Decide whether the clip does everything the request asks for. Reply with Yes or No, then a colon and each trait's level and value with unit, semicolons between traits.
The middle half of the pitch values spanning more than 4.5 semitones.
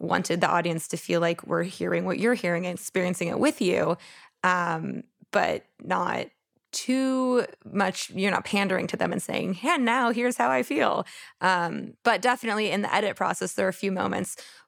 Yes: average, 5.0 semitones